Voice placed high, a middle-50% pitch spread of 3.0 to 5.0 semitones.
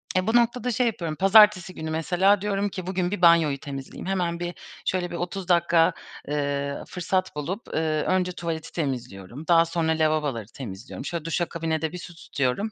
No: medium, 170 Hz; average, 3.3 semitones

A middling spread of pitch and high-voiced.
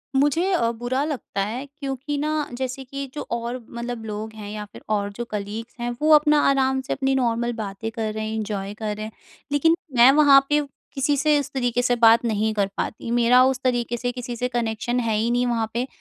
Yes: average, 3.5 semitones; high, 240 Hz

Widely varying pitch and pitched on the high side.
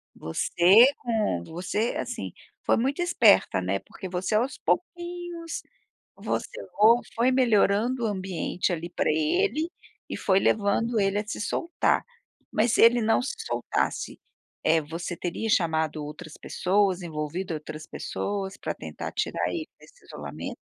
Yes: wide, 5.9 semitones; high, 205 Hz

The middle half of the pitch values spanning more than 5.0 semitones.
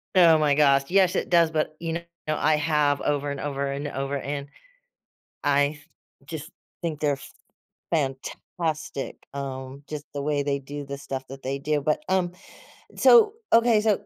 No: narrow, 2.5 semitones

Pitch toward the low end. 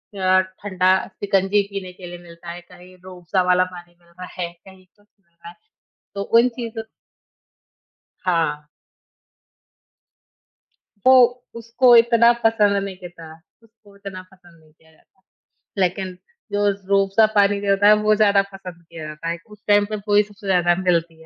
No: high, 190 Hz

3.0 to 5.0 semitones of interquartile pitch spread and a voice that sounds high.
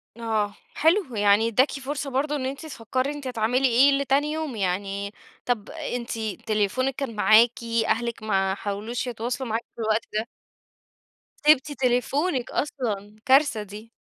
Yes: average, 4.1 semitones; high, 240 Hz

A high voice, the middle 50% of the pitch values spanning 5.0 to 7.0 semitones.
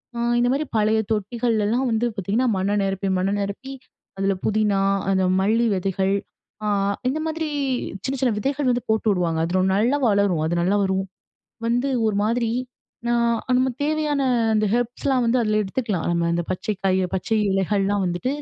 No: high, 215 Hz; average, 4.0 semitones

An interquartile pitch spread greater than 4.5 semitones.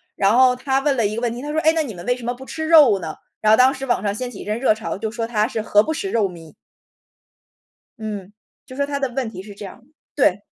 No: average, 4.2 semitones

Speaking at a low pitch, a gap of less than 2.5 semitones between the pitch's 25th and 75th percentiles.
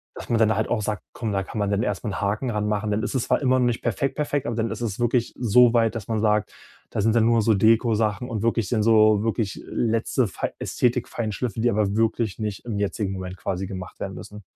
Yes: low, 110 Hz; narrow, 2.1 semitones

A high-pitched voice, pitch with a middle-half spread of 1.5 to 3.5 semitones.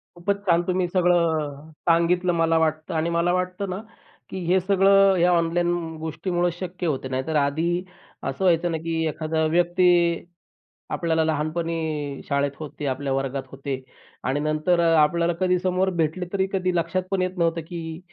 No: medium, 170 Hz; narrow, 2.5 semitones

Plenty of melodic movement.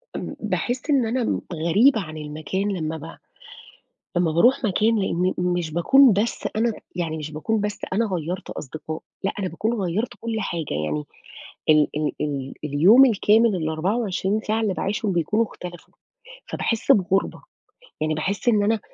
Yes: wide, 5.7 semitones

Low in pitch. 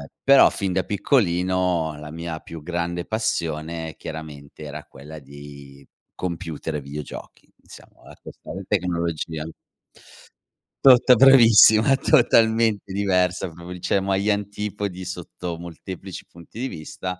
Yes: very low, 90 Hz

